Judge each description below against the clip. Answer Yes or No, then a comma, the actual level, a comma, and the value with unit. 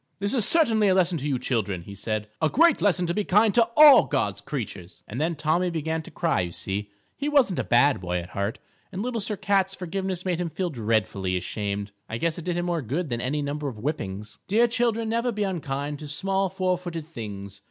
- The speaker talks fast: Yes, fast, 225 wpm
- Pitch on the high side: No, medium, 165 Hz